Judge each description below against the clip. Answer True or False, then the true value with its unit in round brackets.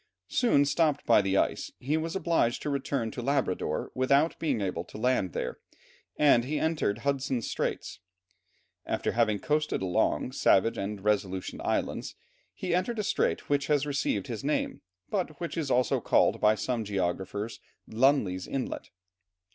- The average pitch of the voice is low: True (130 Hz)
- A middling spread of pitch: False (6.0 semitones)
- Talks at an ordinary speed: True (155 wpm)